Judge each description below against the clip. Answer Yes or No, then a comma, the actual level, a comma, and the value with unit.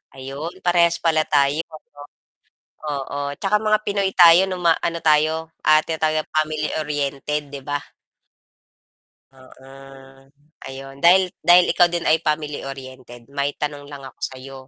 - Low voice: No, medium, 150 Hz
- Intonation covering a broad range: No, average, 3.4 semitones